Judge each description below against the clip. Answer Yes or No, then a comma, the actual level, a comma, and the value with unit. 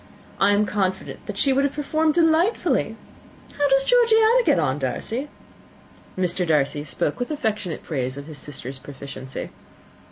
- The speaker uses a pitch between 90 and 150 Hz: No, high, 205 Hz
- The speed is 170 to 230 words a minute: No, average, 150 wpm